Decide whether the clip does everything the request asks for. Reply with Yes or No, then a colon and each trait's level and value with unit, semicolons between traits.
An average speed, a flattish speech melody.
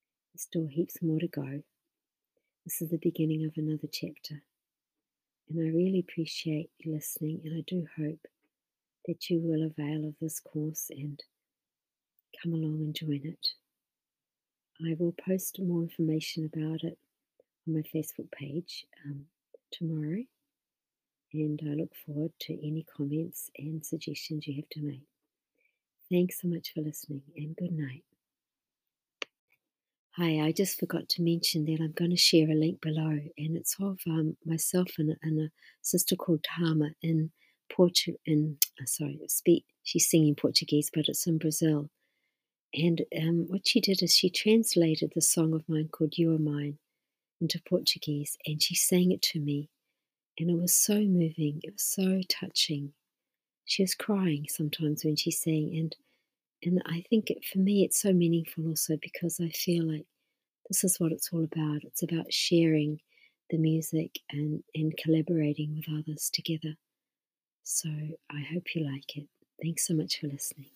Yes: average, 160 wpm; narrow, 2.0 semitones